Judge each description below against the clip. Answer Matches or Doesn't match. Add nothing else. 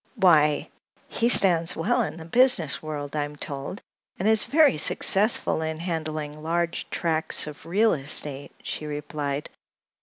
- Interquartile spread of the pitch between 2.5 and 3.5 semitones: Matches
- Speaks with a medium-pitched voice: Matches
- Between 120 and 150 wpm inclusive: Matches